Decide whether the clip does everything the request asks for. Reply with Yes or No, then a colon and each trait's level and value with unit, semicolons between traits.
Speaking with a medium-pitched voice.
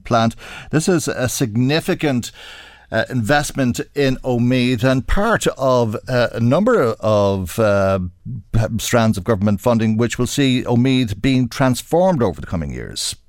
No: low, 120 Hz